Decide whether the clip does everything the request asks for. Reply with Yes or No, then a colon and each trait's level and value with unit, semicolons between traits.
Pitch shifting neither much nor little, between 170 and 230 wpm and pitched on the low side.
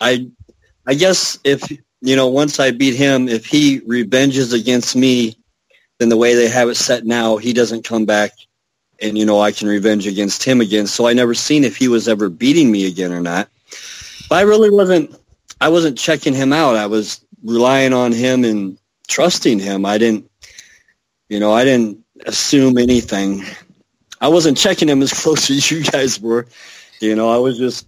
Yes: average, 3.7 semitones; average, 190 wpm; low, 120 Hz